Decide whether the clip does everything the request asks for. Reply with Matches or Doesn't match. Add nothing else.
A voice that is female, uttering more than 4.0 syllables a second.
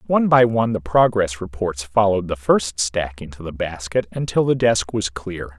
Doesn't match